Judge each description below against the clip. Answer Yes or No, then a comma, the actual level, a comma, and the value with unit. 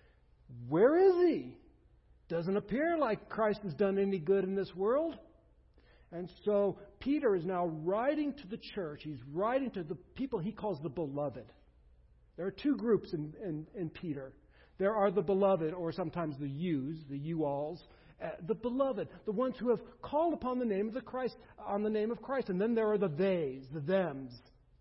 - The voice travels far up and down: Yes, wide, 5.8 semitones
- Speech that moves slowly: No, average, 190 wpm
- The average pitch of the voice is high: Yes, high, 195 Hz